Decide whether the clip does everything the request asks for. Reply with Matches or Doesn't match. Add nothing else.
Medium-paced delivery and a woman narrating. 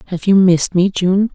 Doesn't match